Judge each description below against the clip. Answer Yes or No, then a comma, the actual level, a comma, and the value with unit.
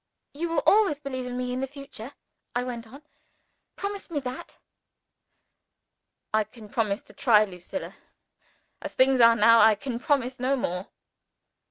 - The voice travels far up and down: No, average, 3.5 semitones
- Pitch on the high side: Yes, very high, 250 Hz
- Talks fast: No, average, 155 wpm